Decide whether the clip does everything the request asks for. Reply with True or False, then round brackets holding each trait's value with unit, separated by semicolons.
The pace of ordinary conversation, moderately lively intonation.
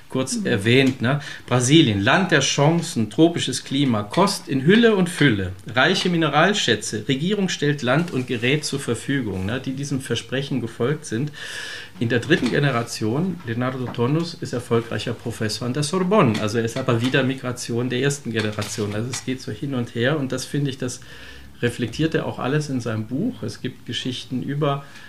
True (175 wpm; 4.0 semitones)